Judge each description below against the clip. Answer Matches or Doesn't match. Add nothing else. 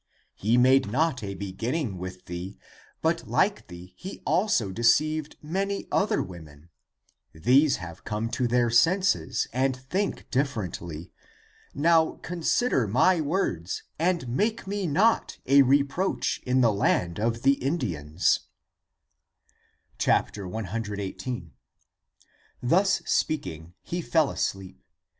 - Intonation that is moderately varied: Doesn't match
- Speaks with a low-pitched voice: Matches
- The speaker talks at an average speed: Doesn't match